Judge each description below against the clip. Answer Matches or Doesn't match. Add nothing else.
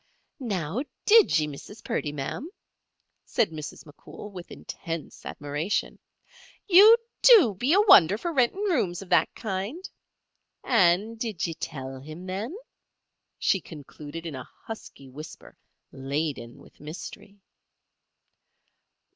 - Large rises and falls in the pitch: Matches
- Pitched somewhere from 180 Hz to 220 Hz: Matches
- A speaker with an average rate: Doesn't match